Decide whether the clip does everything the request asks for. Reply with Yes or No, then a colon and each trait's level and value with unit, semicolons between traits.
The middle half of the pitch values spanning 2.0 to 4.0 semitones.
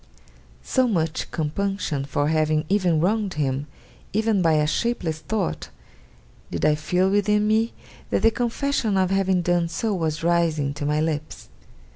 No: average, 5.1 semitones